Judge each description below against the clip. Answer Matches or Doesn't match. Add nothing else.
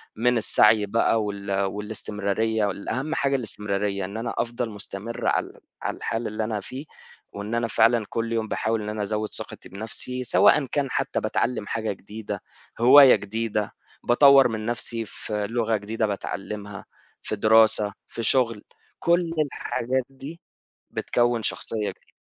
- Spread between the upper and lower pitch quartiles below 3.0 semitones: Matches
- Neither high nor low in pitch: Doesn't match